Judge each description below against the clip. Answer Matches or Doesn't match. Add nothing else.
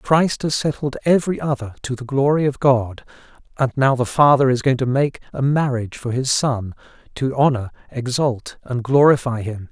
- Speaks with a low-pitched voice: Matches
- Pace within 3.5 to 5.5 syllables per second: Matches